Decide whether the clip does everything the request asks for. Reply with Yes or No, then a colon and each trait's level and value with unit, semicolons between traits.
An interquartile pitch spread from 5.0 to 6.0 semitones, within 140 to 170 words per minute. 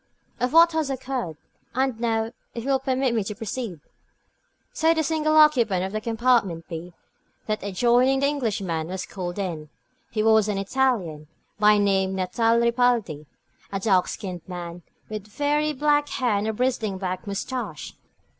Yes: wide, 5.5 semitones; average, 160 wpm